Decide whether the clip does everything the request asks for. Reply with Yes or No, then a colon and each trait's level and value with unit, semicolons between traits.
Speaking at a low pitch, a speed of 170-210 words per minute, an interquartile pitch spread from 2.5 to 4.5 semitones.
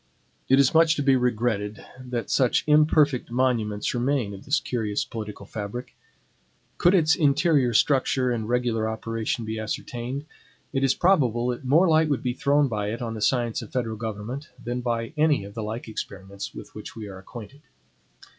Yes: low, 120 Hz; average, 175 wpm; average, 4.1 semitones